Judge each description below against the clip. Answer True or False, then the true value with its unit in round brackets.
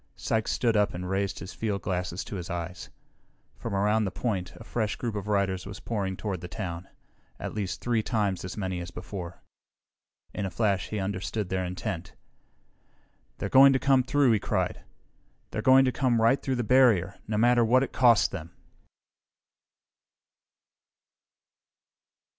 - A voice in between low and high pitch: False (100 Hz)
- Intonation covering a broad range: False (3.8 semitones)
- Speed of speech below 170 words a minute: True (160 wpm)